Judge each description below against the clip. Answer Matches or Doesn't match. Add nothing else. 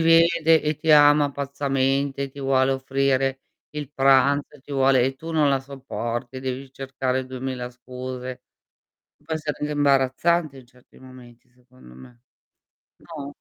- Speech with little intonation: Matches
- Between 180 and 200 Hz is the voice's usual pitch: Doesn't match